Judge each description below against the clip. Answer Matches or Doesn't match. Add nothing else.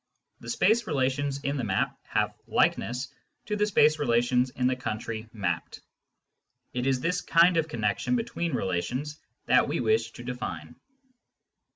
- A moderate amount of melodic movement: Doesn't match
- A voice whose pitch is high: Doesn't match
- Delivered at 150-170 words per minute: Matches